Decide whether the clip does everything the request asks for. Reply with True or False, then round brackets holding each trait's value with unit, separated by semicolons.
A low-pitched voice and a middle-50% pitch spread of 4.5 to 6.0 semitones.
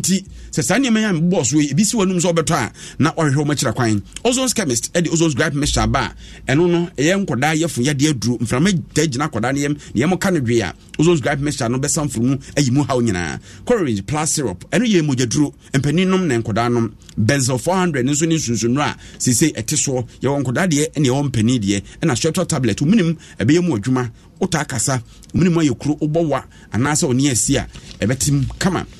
False (145 Hz; 5.5 semitones)